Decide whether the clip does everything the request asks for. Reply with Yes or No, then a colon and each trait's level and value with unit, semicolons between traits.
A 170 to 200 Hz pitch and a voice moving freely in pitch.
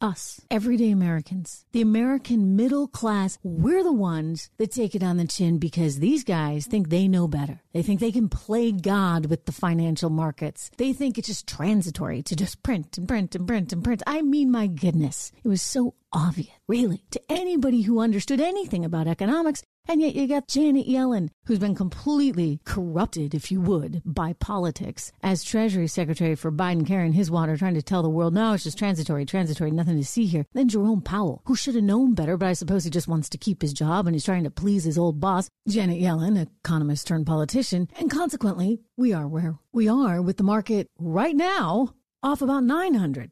Yes: high, 190 Hz; wide, 5.7 semitones